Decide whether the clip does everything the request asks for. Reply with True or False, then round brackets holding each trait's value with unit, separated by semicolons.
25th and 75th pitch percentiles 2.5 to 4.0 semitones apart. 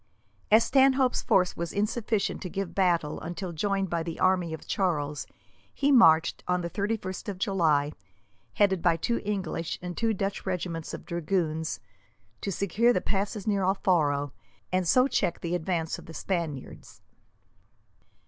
True (3.5 semitones)